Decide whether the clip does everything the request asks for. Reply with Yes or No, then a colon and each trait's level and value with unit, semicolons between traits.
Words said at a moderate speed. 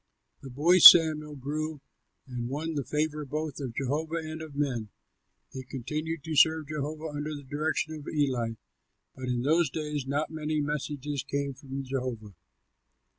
Yes: average, 155 wpm